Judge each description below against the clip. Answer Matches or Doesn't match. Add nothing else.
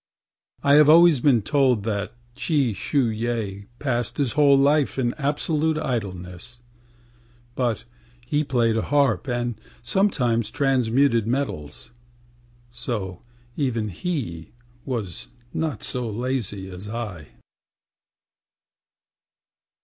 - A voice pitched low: Matches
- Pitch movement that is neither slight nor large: Matches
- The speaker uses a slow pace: Matches